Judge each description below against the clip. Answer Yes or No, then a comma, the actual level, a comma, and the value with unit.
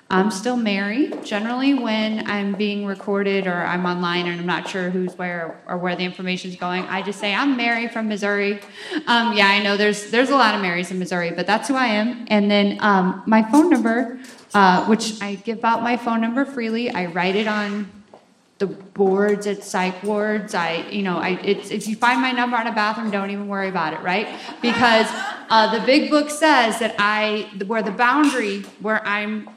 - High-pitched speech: Yes, high, 210 Hz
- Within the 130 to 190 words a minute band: No, fast, 205 wpm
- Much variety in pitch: No, average, 3.0 semitones